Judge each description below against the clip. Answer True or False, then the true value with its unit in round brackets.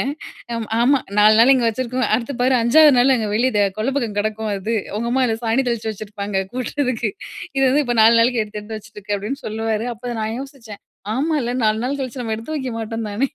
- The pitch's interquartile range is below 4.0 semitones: True (3.0 semitones)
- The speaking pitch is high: True (230 Hz)